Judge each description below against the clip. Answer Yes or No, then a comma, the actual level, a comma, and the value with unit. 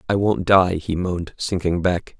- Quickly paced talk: No, average, 190 wpm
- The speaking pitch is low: Yes, very low, 90 Hz